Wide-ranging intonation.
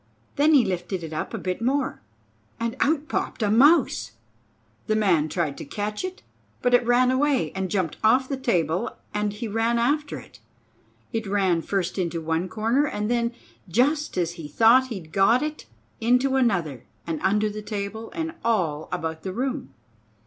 Yes: wide, 6.0 semitones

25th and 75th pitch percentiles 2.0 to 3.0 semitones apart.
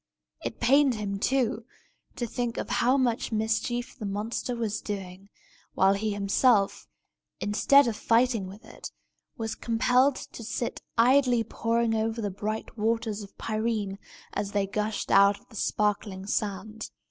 Yes: narrow, 2.6 semitones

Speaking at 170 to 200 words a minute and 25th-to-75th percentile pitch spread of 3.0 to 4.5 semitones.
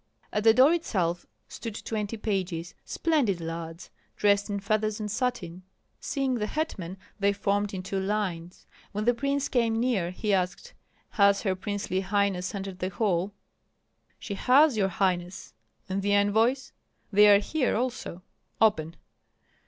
No: average, 145 wpm; average, 3.3 semitones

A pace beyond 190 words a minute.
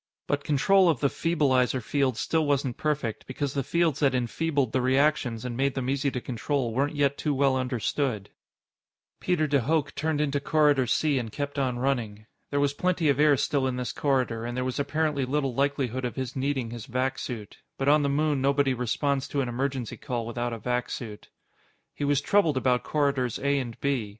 Yes: average, 200 wpm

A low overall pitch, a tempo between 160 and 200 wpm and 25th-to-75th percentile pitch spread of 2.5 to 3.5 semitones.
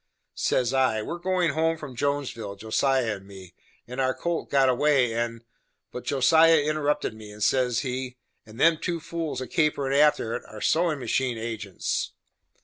No: low, 130 Hz; average, 175 wpm; average, 4.7 semitones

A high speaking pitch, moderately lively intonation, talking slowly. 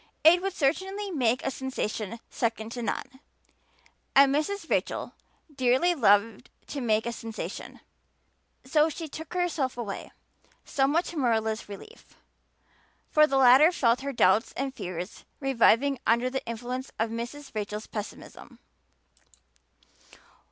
Yes: very high, 260 Hz; average, 4.5 semitones; slow, 125 wpm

